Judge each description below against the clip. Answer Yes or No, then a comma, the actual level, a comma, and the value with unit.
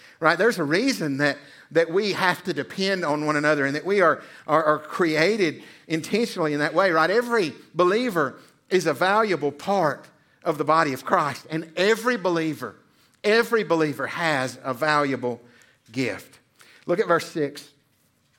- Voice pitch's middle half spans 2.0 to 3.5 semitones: No, average, 4.1 semitones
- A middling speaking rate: Yes, average, 160 wpm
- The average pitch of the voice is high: No, medium, 155 Hz